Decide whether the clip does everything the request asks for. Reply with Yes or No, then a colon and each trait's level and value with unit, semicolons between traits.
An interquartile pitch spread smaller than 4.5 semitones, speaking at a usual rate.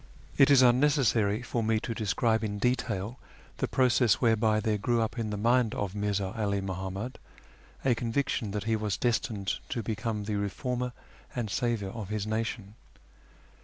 Yes: average, 2.8 semitones; average, 165 wpm